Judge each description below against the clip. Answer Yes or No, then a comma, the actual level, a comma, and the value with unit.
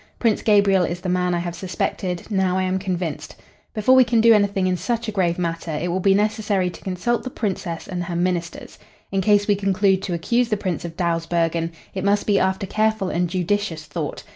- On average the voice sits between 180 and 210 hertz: Yes, medium, 185 Hz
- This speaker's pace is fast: Yes, fast, 215 wpm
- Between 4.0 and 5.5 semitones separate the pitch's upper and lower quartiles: No, average, 2.9 semitones